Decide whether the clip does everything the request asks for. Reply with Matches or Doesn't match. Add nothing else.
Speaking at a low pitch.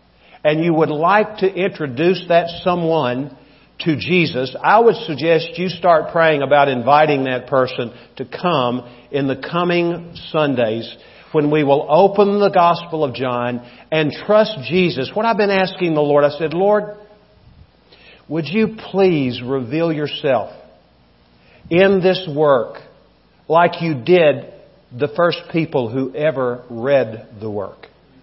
Doesn't match